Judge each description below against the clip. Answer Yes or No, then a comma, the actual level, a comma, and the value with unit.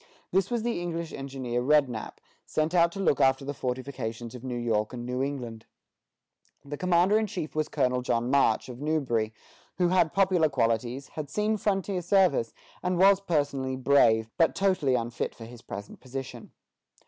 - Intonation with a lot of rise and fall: Yes, wide, 6.1 semitones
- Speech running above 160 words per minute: Yes, average, 170 wpm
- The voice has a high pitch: No, medium, 140 Hz